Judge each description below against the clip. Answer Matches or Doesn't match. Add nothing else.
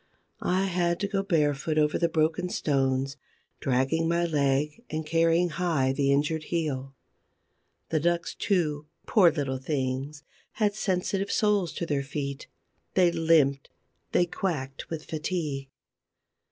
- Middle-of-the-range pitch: Matches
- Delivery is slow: Matches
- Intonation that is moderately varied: Matches